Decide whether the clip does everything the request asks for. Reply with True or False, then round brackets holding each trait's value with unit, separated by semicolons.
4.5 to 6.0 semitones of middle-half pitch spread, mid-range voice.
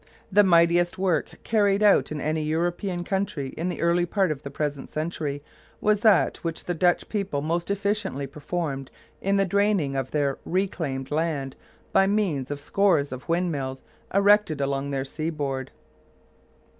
True (5.3 semitones; 165 Hz)